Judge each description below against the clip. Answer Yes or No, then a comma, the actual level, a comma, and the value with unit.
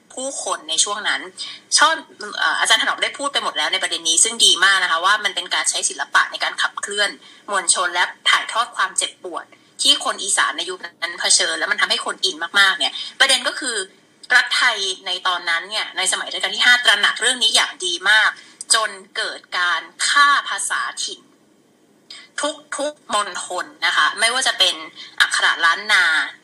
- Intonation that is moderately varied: No, wide, 7.3 semitones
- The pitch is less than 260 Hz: No, very high, 270 Hz